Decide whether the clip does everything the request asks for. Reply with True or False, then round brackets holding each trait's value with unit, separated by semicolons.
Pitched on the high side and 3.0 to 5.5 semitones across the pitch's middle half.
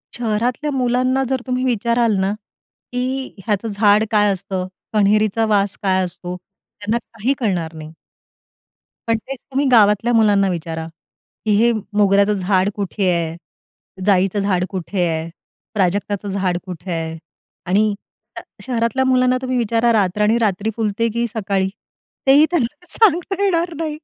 True (210 Hz; 4.2 semitones)